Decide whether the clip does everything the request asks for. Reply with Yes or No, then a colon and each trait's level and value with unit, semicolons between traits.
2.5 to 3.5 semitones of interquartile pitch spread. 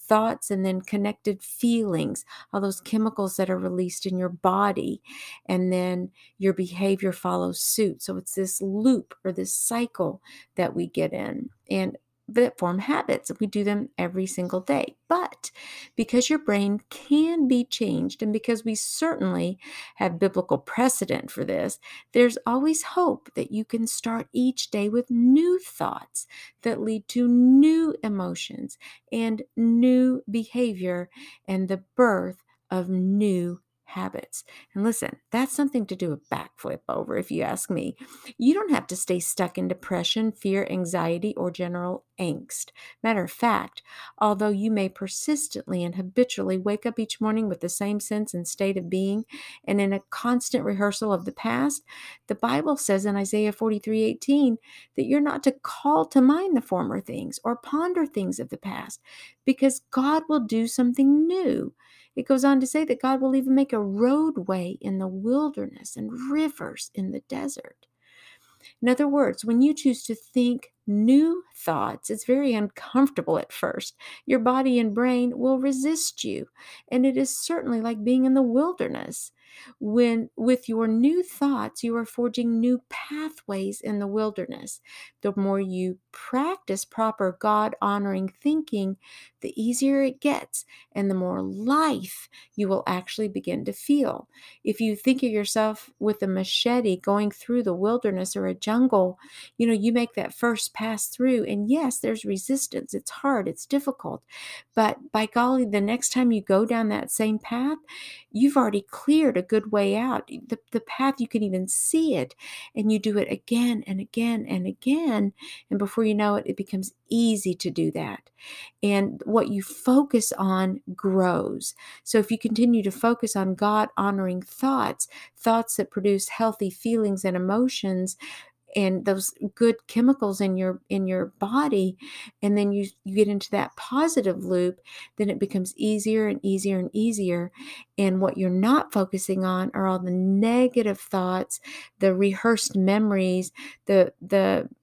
No: average, 4.8 semitones